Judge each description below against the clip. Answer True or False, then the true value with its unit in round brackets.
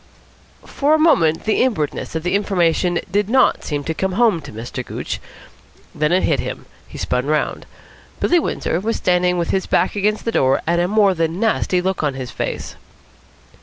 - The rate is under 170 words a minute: False (190 wpm)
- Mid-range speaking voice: True (180 Hz)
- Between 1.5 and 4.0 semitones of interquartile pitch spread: False (4.9 semitones)